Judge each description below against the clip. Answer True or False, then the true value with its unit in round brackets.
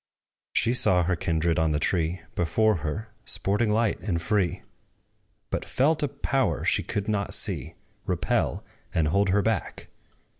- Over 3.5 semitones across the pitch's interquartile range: True (4.8 semitones)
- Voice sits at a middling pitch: False (95 Hz)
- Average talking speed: True (150 wpm)